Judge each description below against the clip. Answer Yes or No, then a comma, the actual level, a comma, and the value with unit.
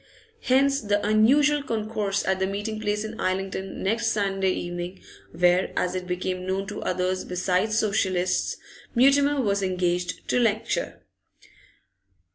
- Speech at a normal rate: No, slow, 130 wpm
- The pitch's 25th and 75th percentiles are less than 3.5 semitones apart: Yes, average, 3.1 semitones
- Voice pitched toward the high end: Yes, high, 200 Hz